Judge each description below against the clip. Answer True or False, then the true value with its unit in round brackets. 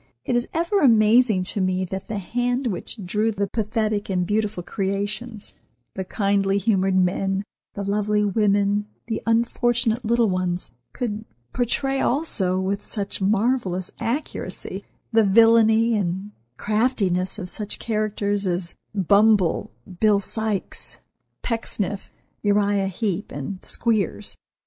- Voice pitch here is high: True (205 Hz)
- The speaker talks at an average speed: False (120 wpm)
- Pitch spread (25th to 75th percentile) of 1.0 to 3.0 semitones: True (2.7 semitones)